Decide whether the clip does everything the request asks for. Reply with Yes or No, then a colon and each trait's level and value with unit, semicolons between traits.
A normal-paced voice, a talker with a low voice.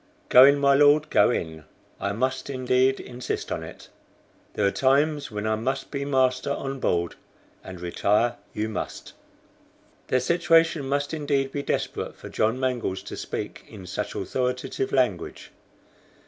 Yes: average, 150 wpm; low, 130 Hz